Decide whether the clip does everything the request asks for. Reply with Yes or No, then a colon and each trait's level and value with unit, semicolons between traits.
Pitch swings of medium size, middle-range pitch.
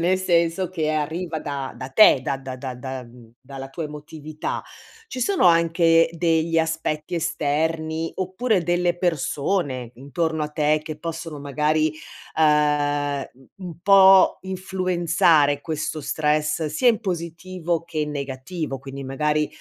Yes: average, 3.0 semitones; medium, 160 Hz